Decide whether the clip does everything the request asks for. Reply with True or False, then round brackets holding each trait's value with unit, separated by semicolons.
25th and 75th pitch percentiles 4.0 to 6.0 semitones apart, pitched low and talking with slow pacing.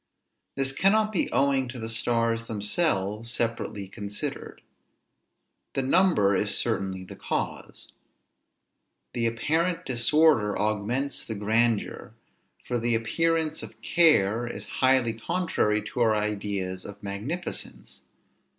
True (5.1 semitones; 115 Hz; 115 wpm)